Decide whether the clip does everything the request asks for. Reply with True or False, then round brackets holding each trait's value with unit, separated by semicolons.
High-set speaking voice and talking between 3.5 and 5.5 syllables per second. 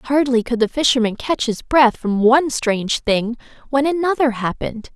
True (250 Hz; 5.0 syllables/s)